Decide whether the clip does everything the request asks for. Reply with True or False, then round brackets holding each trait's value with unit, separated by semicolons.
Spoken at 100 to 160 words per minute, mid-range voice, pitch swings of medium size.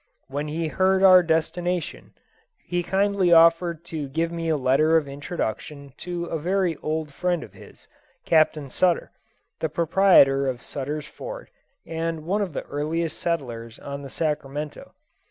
True (150 wpm; 160 Hz; 3.2 semitones)